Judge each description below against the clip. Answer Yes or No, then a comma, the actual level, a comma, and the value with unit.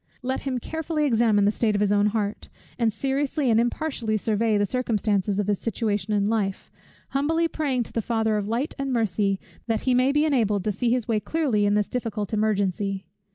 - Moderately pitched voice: No, high, 220 Hz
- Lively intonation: No, average, 3.7 semitones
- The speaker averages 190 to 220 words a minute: Yes, average, 200 wpm